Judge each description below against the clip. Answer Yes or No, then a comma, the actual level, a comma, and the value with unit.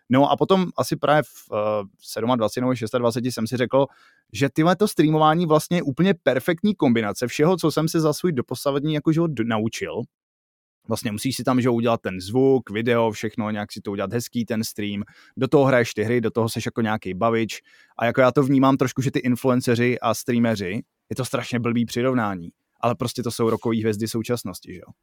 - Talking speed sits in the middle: No, fast, 200 wpm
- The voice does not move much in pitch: No, average, 3.8 semitones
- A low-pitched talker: Yes, low, 120 Hz